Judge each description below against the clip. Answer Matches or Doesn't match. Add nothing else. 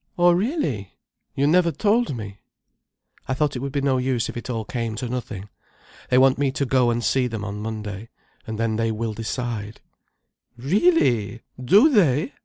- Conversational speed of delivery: Matches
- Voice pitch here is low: Matches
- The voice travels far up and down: Doesn't match